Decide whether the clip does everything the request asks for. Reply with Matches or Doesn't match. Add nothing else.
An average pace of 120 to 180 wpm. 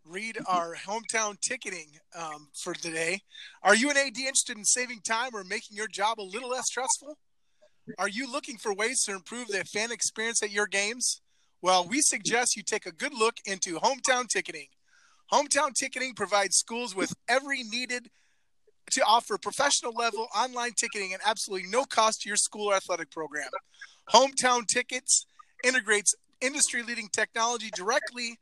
Matches